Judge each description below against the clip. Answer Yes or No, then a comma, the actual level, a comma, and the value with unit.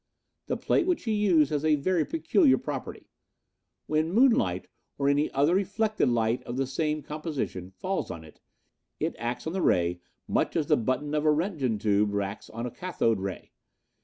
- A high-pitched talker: No, medium, 145 Hz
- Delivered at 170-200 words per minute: Yes, average, 180 wpm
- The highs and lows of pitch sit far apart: Yes, wide, 7.9 semitones